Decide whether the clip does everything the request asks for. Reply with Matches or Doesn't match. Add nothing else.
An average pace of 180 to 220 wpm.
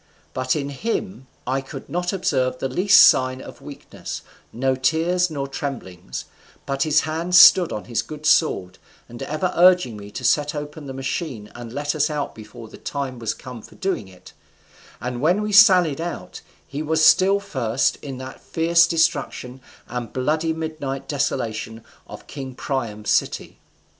Doesn't match